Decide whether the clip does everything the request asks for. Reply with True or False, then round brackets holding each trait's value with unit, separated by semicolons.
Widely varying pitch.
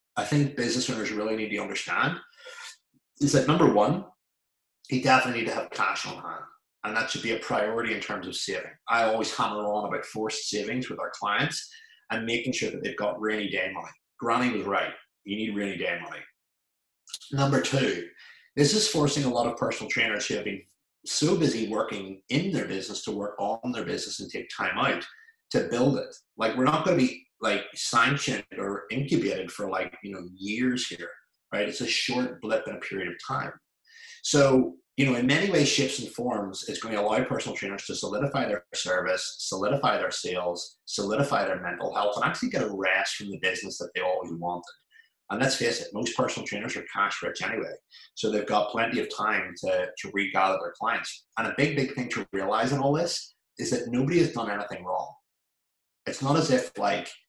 True (6.3 semitones)